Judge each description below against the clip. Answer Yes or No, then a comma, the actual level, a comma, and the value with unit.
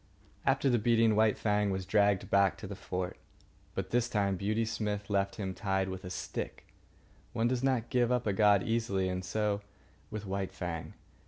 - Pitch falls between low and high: No, low, 105 Hz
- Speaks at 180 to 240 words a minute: Yes, average, 185 wpm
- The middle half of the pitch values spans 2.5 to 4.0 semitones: Yes, average, 2.9 semitones